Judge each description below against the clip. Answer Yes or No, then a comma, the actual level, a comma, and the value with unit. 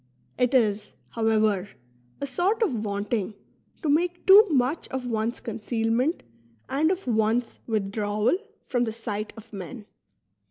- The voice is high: Yes, high, 230 Hz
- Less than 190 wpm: Yes, slow, 135 wpm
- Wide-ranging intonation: No, average, 4.1 semitones